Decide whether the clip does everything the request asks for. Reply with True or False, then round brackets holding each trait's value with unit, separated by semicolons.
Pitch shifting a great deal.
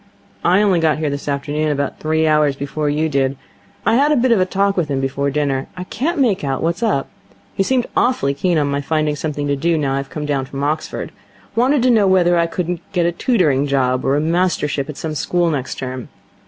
False (4.6 semitones)